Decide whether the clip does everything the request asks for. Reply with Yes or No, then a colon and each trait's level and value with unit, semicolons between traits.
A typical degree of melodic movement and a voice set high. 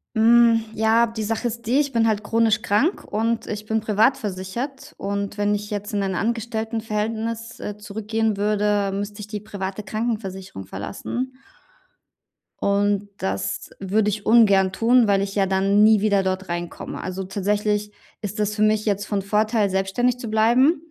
No: narrow, 2.1 semitones; high, 210 Hz